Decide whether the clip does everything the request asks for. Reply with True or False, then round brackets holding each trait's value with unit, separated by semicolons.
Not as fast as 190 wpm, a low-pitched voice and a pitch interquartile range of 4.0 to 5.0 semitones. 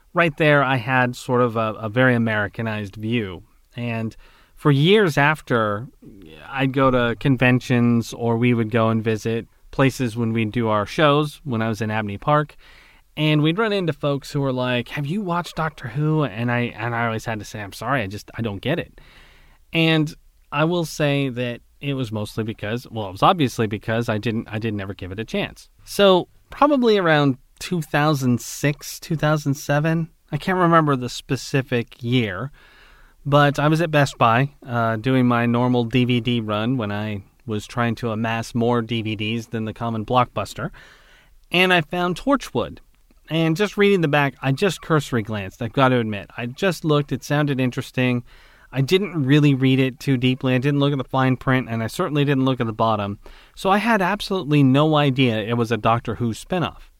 False (195 wpm; 130 Hz; 4.6 semitones)